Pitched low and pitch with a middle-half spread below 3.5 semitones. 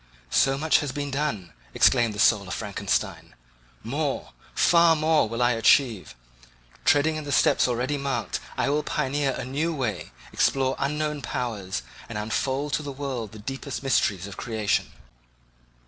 No: low, 130 Hz; average, 5.0 semitones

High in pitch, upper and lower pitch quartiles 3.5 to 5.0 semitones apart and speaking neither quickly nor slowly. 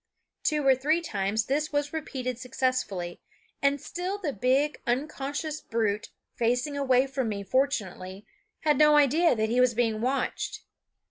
Yes: very high, 260 Hz; average, 4.4 semitones; average, 145 wpm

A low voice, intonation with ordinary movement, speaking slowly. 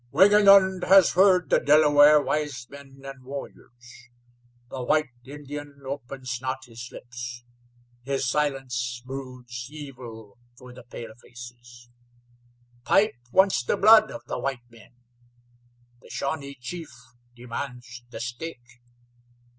Yes: low, 130 Hz; average, 3.4 semitones; slow, 115 wpm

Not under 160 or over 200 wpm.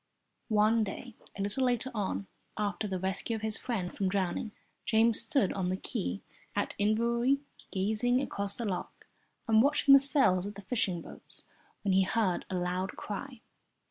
Yes: average, 170 wpm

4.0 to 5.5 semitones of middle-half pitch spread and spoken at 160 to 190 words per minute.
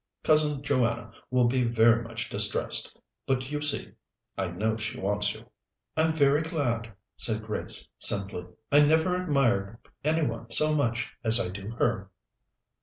No: average, 4.8 semitones; average, 150 wpm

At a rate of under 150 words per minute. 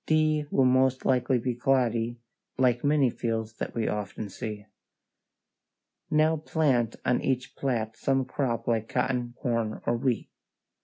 Yes: average, 140 wpm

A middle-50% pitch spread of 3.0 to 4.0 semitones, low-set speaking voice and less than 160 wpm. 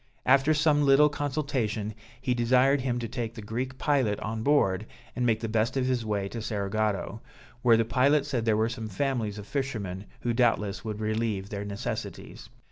No: average, 3.5 semitones; low, 115 Hz; average, 185 wpm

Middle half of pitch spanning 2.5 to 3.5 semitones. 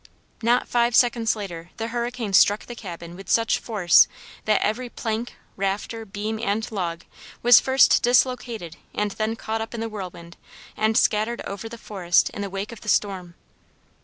Yes: average, 3.1 semitones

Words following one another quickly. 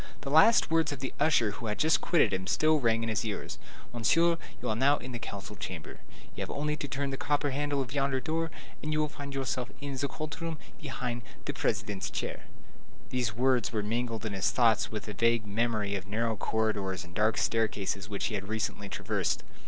Yes: fast, 215 wpm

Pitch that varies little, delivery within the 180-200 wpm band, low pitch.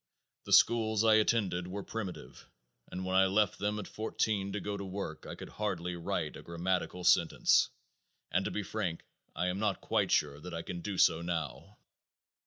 No: average, 3.1 semitones; average, 190 wpm; very low, 95 Hz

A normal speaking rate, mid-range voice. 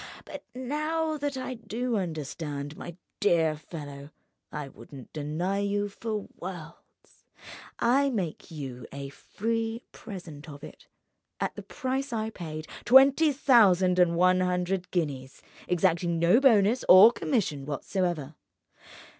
No: slow, 120 wpm; medium, 180 Hz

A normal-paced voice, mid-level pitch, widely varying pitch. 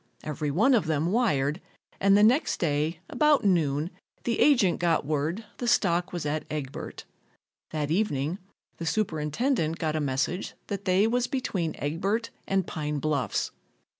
Yes: average, 150 wpm; medium, 170 Hz; wide, 5.8 semitones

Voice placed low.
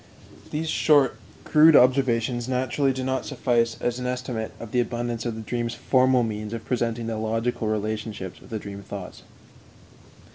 Yes: low, 120 Hz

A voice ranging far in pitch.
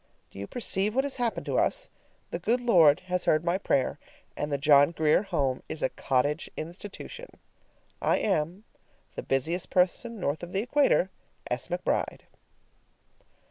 Yes: wide, 6.1 semitones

